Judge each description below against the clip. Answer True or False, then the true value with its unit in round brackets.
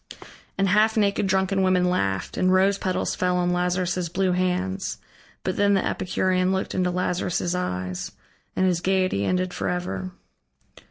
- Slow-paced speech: False (150 wpm)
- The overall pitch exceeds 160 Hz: True (185 Hz)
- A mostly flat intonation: True (1.1 semitones)